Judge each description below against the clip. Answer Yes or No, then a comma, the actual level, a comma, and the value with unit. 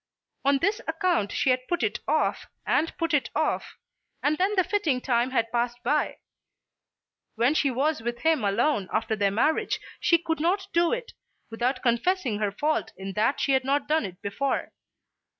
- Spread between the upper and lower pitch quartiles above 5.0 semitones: Yes, wide, 5.4 semitones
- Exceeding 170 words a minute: Yes, average, 180 wpm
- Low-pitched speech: No, very high, 270 Hz